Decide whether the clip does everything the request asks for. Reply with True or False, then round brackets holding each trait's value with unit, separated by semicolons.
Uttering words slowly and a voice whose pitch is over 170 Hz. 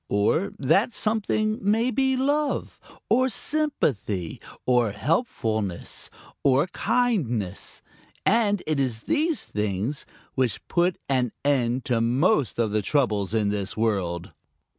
False (120 wpm; 135 Hz)